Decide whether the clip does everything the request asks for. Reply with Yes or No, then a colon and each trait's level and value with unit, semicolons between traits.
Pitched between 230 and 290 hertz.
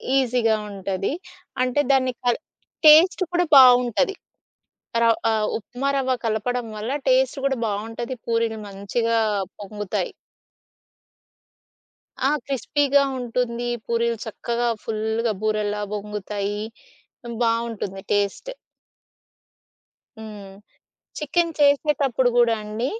Yes: high, 235 Hz